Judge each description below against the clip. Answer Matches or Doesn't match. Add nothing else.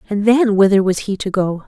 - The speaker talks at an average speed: Doesn't match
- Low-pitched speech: Doesn't match